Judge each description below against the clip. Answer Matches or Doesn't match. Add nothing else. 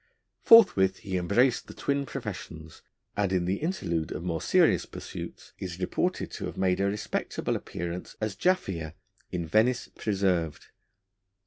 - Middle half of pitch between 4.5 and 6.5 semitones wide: Doesn't match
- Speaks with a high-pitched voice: Doesn't match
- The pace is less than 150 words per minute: Matches